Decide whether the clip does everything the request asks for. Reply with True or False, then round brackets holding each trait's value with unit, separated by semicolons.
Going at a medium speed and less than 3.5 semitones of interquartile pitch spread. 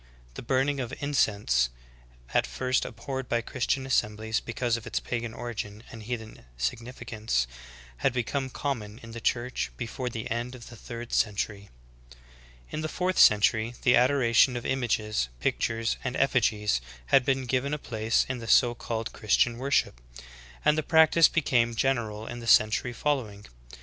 True (170 wpm; 3.1 semitones)